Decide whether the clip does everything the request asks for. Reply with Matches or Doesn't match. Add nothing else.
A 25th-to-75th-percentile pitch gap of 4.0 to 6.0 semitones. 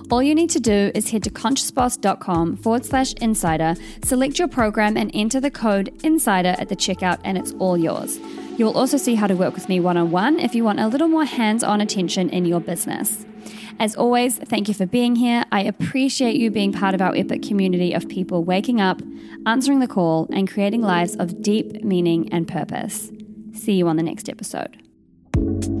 Matches